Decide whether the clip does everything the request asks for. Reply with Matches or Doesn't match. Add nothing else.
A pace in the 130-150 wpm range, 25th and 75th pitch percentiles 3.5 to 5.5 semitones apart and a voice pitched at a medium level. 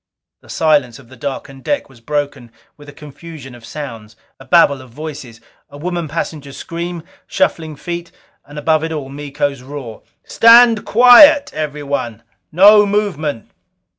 Matches